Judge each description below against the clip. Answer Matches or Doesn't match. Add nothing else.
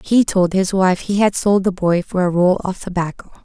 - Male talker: Doesn't match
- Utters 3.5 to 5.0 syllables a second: Matches